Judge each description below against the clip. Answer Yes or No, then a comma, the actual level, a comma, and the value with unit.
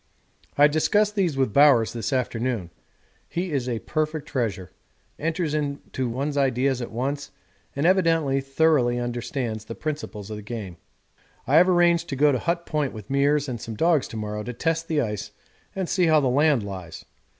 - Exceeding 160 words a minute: Yes, average, 180 wpm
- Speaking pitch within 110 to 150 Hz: Yes, medium, 140 Hz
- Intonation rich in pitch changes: No, average, 5.0 semitones